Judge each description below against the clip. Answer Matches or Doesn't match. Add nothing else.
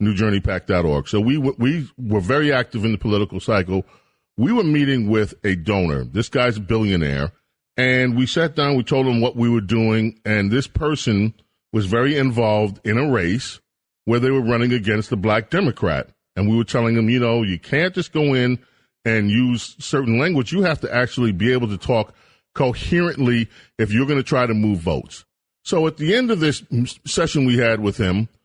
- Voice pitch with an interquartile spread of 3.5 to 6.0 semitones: Matches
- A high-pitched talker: Doesn't match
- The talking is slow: Doesn't match